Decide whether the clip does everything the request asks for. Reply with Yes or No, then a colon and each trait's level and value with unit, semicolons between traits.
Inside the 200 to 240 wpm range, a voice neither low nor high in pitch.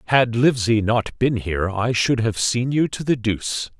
No: fast, 205 wpm; low, 115 Hz